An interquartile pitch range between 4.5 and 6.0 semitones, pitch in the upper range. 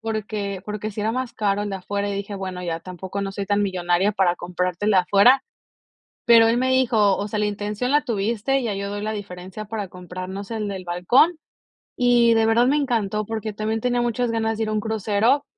No: narrow, 2.6 semitones; high, 210 Hz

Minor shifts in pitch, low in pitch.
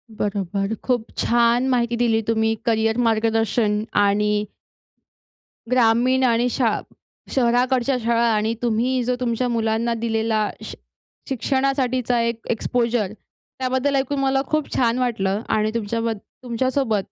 No: narrow, 2.2 semitones; high, 235 Hz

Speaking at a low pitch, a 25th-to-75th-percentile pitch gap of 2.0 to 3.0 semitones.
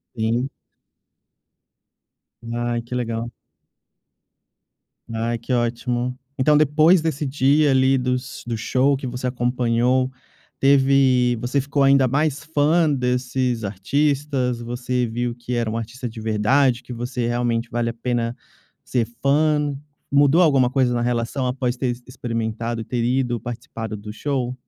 Yes: low, 125 Hz; narrow, 2.4 semitones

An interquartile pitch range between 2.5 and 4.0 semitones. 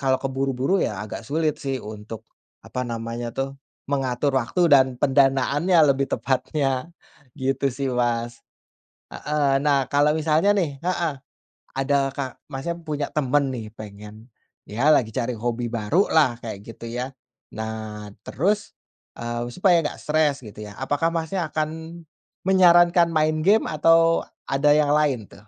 No: average, 4.4 semitones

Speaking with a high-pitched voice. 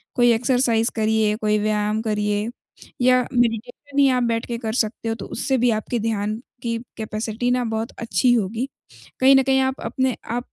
Yes: high, 230 Hz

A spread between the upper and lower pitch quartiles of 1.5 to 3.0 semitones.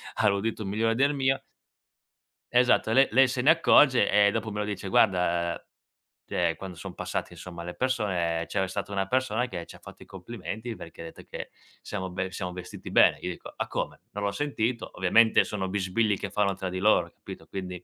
No: average, 3.8 semitones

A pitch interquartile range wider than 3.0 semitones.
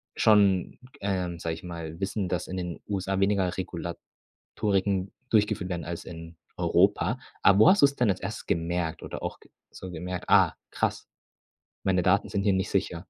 No: narrow, 2.4 semitones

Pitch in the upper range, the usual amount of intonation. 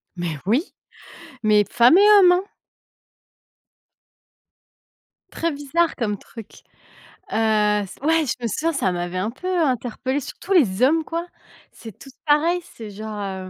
No: high, 245 Hz; wide, 7.7 semitones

